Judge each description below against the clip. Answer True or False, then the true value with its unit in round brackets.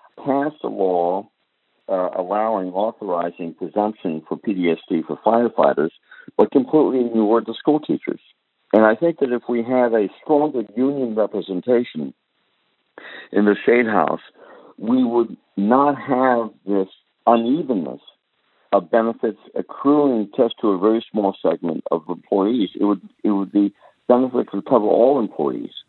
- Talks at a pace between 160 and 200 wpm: False (140 wpm)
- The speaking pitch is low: True (115 Hz)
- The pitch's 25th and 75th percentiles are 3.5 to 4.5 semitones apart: True (4.2 semitones)